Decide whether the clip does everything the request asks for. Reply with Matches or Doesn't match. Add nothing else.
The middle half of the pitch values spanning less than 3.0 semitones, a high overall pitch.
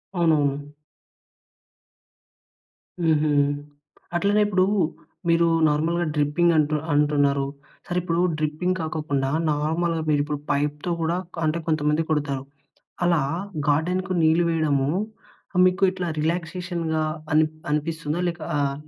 Doesn't match